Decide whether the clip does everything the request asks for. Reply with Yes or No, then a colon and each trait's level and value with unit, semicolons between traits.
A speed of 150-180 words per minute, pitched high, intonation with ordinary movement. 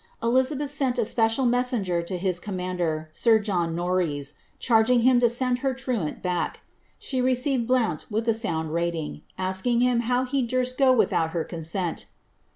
No: average, 175 wpm; high, 225 Hz; wide, 6.3 semitones